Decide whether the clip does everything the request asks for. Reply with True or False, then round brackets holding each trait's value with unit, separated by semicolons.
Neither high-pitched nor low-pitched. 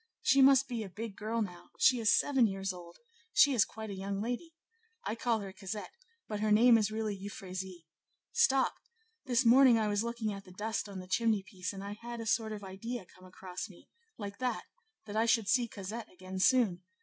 False (215 Hz)